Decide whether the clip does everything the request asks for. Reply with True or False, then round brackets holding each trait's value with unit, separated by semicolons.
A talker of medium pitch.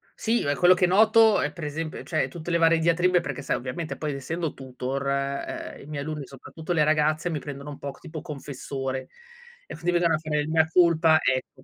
True (155 Hz)